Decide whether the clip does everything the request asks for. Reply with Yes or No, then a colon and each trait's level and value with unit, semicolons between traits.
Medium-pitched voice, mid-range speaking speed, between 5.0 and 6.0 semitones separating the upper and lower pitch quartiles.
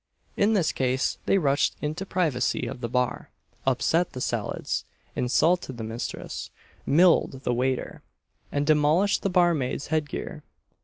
Yes: medium, 145 Hz; average, 145 wpm; wide, 5.4 semitones